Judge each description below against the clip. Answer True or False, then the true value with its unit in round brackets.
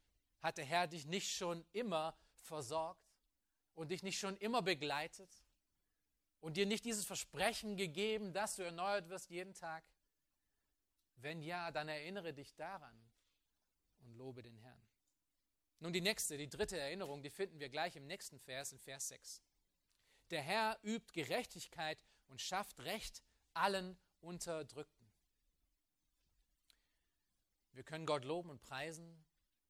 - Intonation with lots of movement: True (5.8 semitones)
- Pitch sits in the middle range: True (160 Hz)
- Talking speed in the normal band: True (135 wpm)